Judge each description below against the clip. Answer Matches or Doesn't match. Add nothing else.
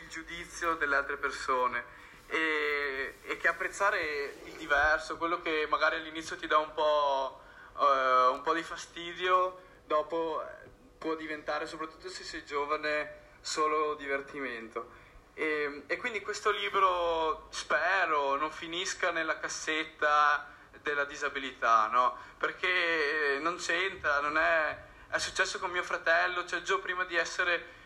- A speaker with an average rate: Matches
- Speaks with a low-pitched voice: Doesn't match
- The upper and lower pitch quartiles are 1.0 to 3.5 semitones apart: Matches